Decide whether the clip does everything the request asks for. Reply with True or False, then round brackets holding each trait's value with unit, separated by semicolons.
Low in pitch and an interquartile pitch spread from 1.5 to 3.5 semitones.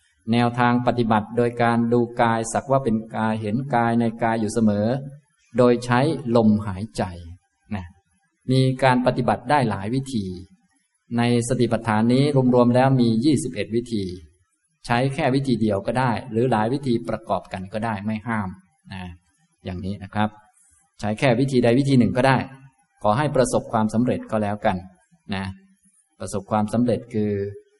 True (115 Hz; 3.2 semitones)